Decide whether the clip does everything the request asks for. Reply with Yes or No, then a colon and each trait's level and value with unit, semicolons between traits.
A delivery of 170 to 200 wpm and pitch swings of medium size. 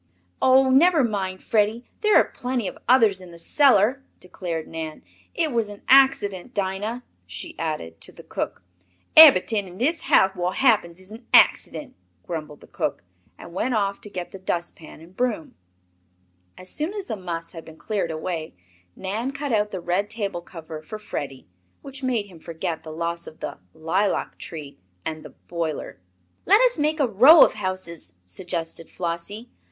No: average, 175 wpm; wide, 6.5 semitones